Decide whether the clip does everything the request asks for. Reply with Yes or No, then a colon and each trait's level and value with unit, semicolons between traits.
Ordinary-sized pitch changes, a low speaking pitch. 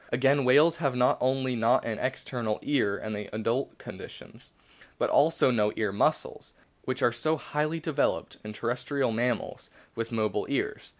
Yes: average, 3.7 semitones; low, 125 Hz